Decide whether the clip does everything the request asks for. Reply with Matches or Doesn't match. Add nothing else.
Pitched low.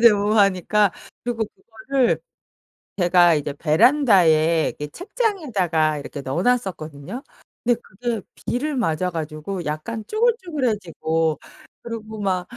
Doesn't match